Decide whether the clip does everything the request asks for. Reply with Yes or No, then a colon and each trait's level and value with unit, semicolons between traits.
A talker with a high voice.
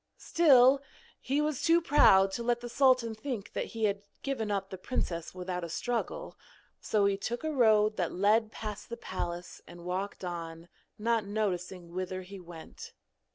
Yes: high, 210 Hz